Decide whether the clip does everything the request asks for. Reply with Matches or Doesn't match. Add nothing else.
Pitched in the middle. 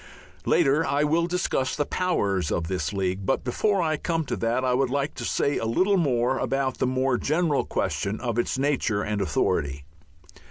Doesn't match